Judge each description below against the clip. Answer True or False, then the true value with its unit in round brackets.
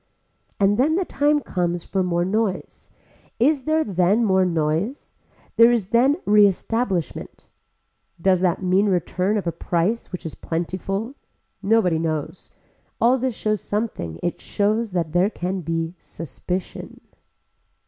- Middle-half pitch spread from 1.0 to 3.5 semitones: False (4.5 semitones)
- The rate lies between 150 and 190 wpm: False (135 wpm)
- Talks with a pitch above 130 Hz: True (190 Hz)